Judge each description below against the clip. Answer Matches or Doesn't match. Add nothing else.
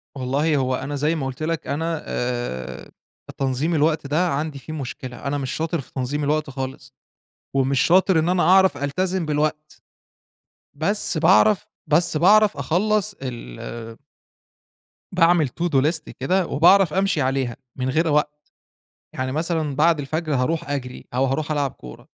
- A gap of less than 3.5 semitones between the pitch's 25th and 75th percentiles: Doesn't match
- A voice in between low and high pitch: Matches